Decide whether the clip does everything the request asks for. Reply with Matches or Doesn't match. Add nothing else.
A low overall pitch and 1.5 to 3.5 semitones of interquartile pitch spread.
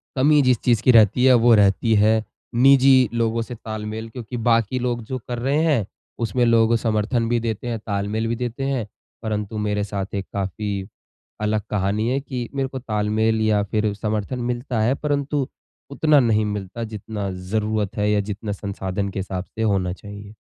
Matches